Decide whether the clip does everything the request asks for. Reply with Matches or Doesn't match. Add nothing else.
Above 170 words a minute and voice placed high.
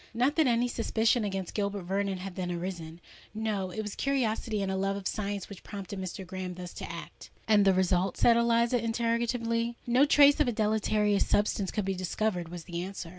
Matches